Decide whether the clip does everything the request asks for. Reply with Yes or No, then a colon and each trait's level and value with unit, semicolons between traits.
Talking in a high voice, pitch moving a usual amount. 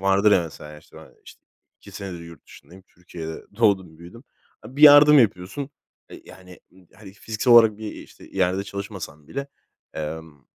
No: very low, 95 Hz; average, 4.6 semitones